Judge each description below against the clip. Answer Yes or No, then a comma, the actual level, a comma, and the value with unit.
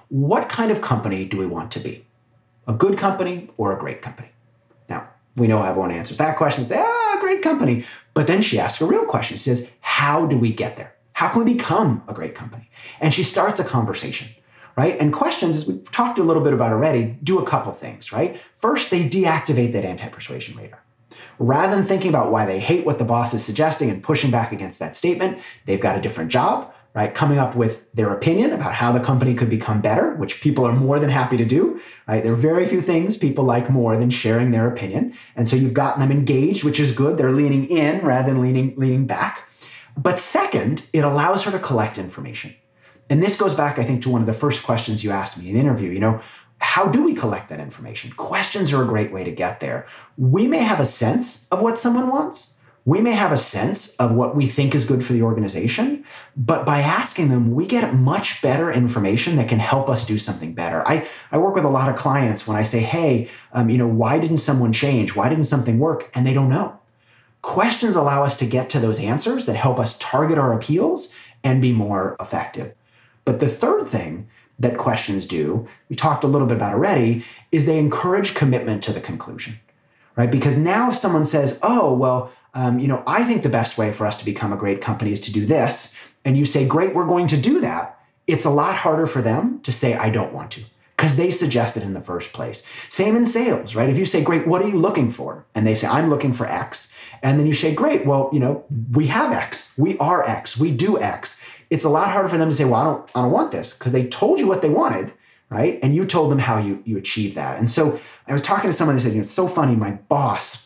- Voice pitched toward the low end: Yes, low, 130 Hz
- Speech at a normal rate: No, fast, 235 wpm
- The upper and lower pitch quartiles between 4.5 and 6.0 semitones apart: Yes, average, 5.2 semitones